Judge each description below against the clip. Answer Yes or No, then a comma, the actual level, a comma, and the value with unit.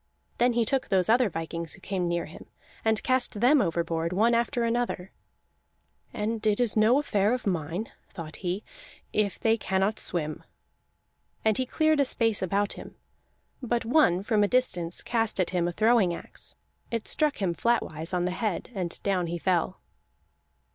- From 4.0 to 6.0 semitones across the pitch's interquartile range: Yes, average, 4.9 semitones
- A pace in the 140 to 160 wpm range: No, average, 170 wpm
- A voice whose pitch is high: Yes, high, 205 Hz